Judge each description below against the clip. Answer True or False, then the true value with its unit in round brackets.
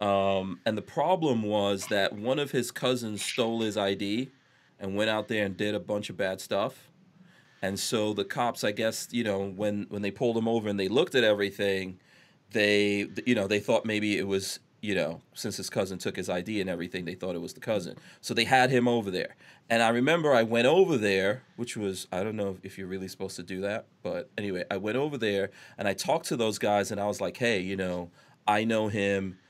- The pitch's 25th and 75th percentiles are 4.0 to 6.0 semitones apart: False (3.0 semitones)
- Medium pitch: False (105 Hz)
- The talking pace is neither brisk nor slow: False (230 wpm)